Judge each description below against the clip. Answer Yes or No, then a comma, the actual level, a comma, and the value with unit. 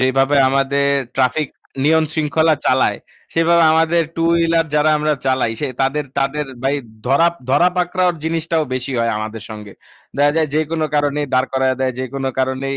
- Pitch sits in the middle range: Yes, medium, 145 Hz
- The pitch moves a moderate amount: Yes, average, 3.4 semitones